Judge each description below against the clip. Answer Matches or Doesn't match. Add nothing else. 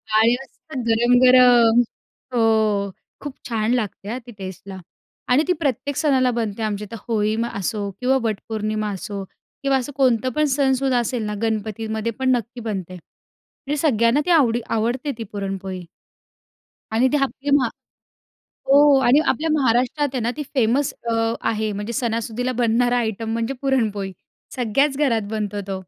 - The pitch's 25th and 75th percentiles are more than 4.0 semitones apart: Doesn't match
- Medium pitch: Doesn't match